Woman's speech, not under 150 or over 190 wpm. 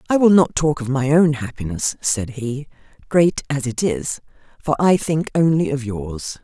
Yes: female; average, 185 wpm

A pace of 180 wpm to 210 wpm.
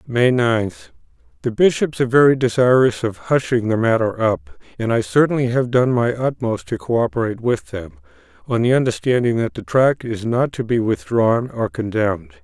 No: average, 170 wpm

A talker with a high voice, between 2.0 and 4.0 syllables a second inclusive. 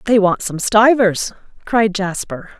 Yes: high, 205 Hz; 3.9 syllables/s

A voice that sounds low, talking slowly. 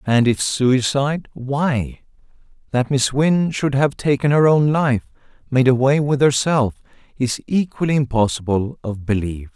Yes: low, 130 Hz; slow, 130 wpm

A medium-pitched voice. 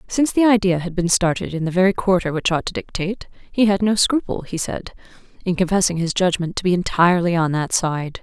Yes: medium, 180 Hz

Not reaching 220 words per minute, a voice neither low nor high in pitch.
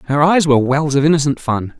No: fast, 235 wpm; medium, 145 Hz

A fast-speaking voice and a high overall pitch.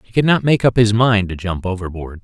No: fast, 270 wpm; low, 105 Hz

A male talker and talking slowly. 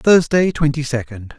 Yes: male; slow, 130 wpm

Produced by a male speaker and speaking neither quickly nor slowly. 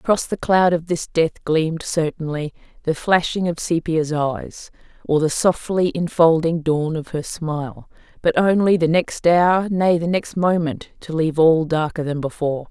No: female; average, 170 wpm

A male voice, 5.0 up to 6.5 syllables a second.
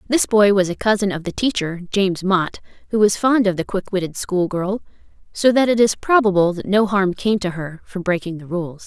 No: female; 5.3 syllables/s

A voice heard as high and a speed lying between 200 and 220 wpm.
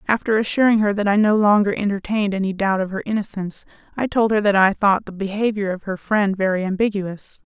Yes: high, 200 Hz; fast, 205 wpm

